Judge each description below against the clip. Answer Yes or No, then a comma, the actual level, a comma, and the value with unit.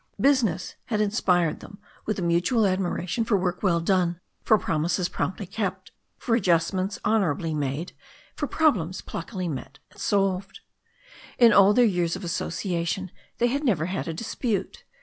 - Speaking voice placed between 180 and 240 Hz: Yes, medium, 185 Hz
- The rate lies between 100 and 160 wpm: Yes, average, 150 wpm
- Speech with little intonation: No, average, 3.8 semitones